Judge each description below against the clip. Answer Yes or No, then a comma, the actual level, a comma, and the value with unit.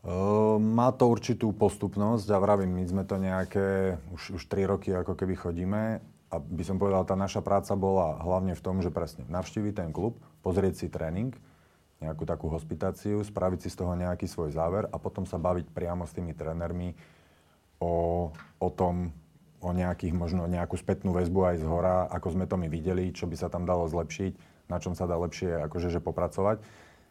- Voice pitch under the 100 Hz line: Yes, very low, 90 Hz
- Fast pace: Yes, fast, 195 wpm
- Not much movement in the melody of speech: Yes, narrow, 2.1 semitones